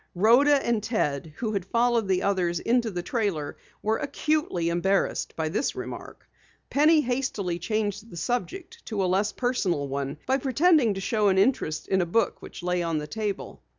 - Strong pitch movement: Yes, wide, 5.8 semitones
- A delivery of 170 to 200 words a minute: Yes, average, 180 wpm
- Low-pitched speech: No, high, 210 Hz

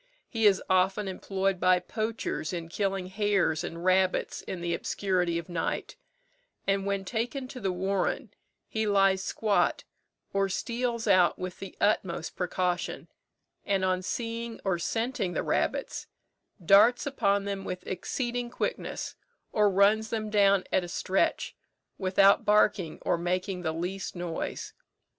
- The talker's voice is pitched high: Yes, high, 195 Hz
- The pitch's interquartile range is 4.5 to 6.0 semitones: No, narrow, 2.6 semitones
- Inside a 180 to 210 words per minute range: No, average, 140 wpm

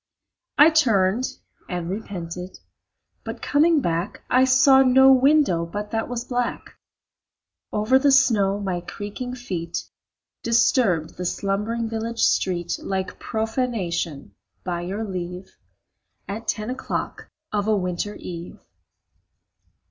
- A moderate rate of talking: No, slow, 115 wpm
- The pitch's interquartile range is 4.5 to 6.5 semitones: Yes, wide, 5.6 semitones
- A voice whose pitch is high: Yes, high, 210 Hz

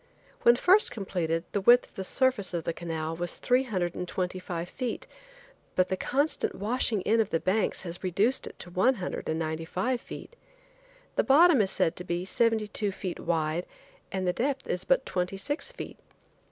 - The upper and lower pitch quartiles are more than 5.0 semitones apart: Yes, wide, 5.6 semitones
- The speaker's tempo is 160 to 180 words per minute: No, average, 195 wpm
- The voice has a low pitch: No, high, 190 Hz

